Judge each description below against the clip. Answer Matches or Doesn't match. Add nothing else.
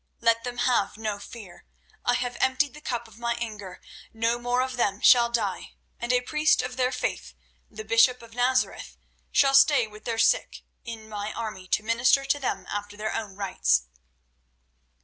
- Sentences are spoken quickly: Doesn't match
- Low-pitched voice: Doesn't match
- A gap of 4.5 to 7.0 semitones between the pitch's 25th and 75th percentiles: Doesn't match